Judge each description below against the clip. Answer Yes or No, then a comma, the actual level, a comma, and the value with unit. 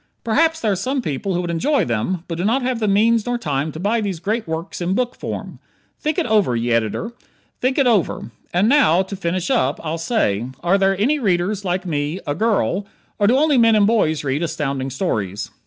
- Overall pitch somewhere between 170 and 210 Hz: Yes, high, 190 Hz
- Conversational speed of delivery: No, fast, 220 wpm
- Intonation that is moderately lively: No, wide, 6.2 semitones